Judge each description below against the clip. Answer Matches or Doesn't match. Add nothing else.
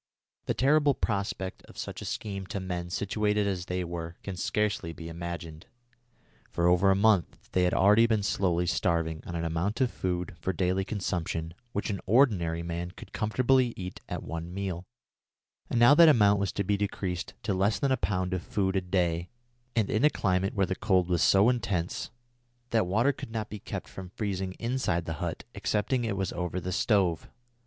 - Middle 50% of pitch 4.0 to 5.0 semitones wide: Doesn't match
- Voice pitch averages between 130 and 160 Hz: Doesn't match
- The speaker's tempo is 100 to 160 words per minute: Doesn't match